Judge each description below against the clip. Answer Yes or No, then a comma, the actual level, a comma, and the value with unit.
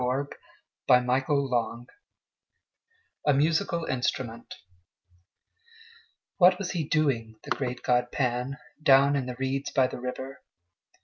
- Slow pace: Yes, slow, 115 wpm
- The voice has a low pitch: Yes, low, 130 Hz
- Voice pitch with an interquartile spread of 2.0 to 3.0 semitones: Yes, narrow, 2.4 semitones